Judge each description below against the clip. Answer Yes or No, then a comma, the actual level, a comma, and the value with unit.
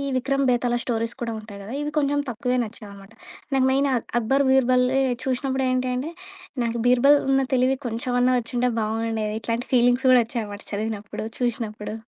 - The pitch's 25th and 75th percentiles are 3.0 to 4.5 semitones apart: No, narrow, 2.6 semitones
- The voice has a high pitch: Yes, high, 245 Hz